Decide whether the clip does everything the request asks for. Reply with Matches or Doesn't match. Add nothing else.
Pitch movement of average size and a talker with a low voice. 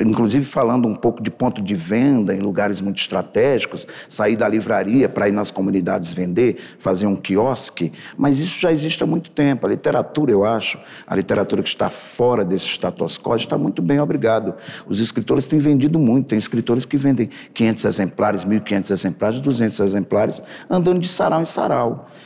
Doesn't match